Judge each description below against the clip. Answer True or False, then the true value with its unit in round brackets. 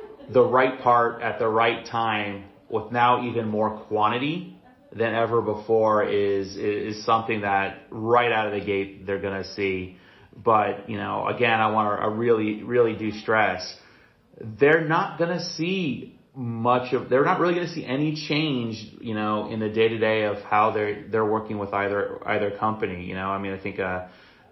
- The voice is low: True (110 Hz)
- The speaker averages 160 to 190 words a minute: True (175 wpm)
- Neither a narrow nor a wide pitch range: True (3.0 semitones)